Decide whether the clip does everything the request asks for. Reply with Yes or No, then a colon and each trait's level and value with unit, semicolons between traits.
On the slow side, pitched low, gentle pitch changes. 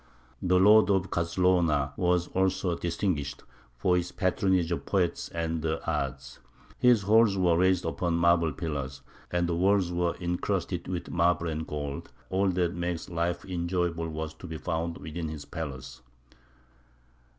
No: average, 150 wpm; very low, 85 Hz; narrow, 2.2 semitones